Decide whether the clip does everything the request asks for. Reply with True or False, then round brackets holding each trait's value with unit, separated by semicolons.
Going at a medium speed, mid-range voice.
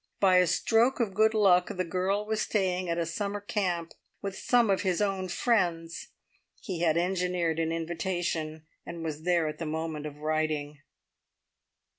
True (165 wpm; 180 Hz)